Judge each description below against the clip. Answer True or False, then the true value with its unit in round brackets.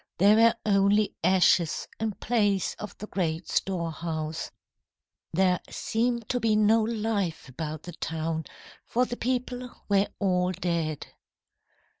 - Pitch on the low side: False (195 Hz)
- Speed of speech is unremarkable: False (125 wpm)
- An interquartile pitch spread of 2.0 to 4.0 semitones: False (4.7 semitones)